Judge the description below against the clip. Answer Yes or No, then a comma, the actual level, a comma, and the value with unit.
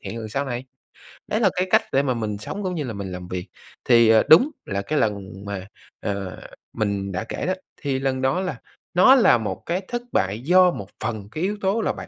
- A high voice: No, low, 120 Hz